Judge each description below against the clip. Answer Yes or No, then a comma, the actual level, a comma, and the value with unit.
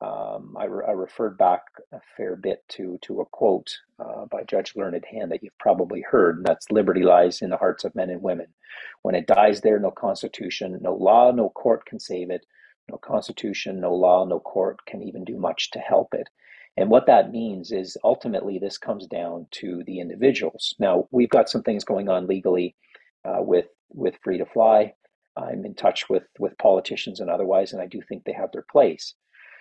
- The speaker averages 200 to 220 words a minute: Yes, fast, 205 wpm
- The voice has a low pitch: Yes, very low, 90 Hz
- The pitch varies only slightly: No, average, 3.7 semitones